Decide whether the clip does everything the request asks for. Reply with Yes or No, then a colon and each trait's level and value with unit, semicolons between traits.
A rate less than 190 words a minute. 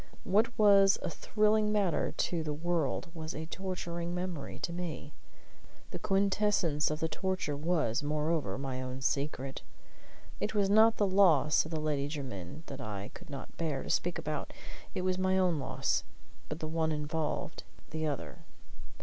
Yes: average, 165 wpm